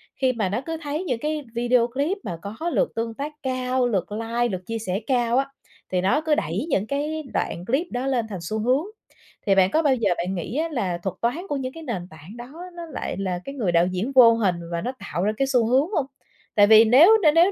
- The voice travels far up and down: Yes, wide, 5.9 semitones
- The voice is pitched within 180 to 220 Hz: No, high, 240 Hz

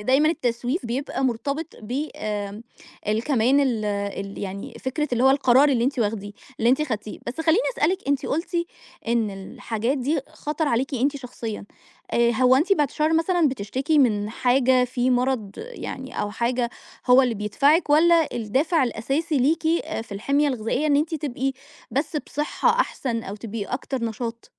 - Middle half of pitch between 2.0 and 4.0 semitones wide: No, average, 4.4 semitones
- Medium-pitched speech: No, very high, 255 Hz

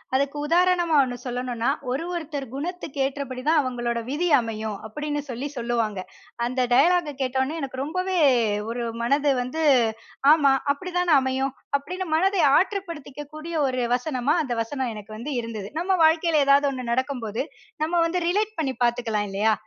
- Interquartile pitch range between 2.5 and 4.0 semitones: No, average, 4.8 semitones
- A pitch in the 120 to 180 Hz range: No, very high, 275 Hz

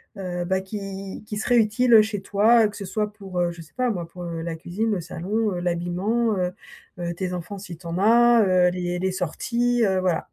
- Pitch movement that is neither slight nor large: Yes, average, 3.4 semitones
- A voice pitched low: No, high, 190 Hz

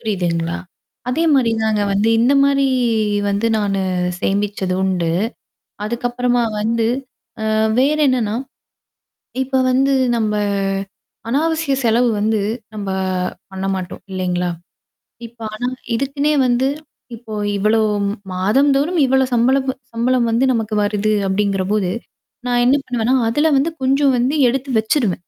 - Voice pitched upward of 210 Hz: Yes, high, 230 Hz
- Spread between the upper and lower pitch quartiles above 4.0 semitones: Yes, average, 4.4 semitones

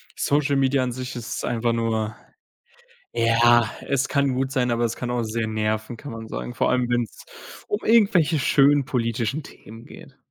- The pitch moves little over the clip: No, average, 3.2 semitones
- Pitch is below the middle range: Yes, low, 120 Hz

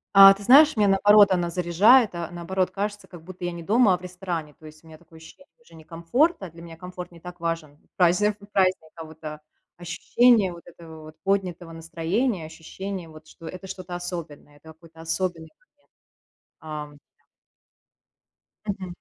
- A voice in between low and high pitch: Yes, medium, 175 Hz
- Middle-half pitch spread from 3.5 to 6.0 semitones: No, average, 3.0 semitones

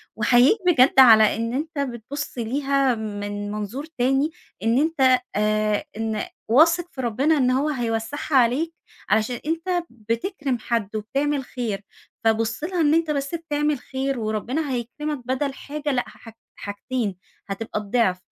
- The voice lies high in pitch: Yes, very high, 255 Hz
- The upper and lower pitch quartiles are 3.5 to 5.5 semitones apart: Yes, average, 4.7 semitones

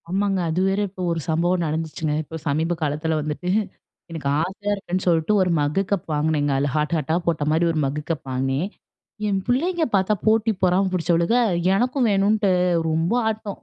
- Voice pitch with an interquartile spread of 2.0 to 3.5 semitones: No, average, 4.2 semitones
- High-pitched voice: No, medium, 170 Hz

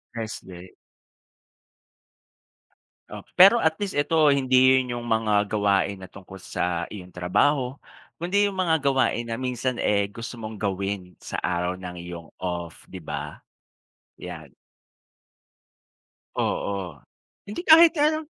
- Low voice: Yes, low, 105 Hz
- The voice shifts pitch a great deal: Yes, wide, 7.4 semitones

